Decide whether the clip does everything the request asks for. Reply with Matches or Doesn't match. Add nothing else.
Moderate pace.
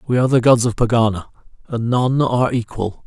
Matches